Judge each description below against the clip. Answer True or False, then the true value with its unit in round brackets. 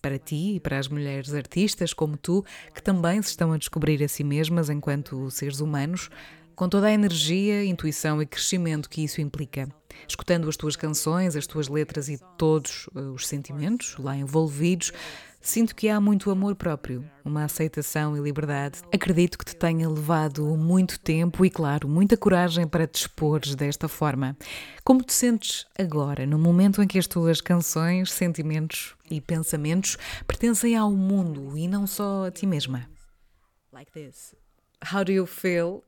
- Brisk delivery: False (155 wpm)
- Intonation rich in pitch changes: False (3.9 semitones)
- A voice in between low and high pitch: True (160 Hz)